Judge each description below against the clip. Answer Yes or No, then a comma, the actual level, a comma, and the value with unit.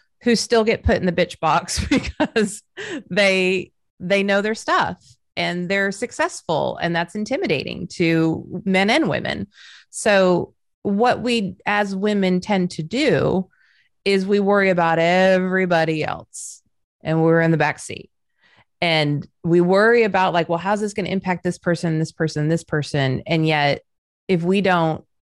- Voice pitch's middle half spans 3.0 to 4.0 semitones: Yes, average, 3.7 semitones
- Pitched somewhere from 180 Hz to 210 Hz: Yes, medium, 185 Hz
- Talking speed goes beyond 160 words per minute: No, average, 155 wpm